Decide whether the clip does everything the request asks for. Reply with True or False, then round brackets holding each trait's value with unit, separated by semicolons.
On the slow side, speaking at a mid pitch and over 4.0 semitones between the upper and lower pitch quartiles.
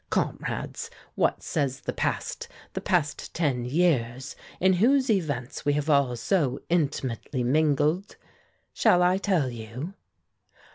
True (125 wpm; 150 Hz; 5.6 semitones)